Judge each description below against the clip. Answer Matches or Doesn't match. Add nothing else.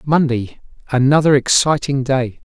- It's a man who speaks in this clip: Matches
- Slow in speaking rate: Matches